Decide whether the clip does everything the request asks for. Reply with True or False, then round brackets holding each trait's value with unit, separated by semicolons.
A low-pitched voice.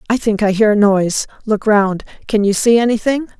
False (215 Hz)